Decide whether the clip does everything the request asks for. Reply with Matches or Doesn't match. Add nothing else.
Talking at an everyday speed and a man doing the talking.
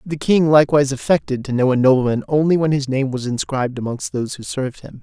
Doesn't match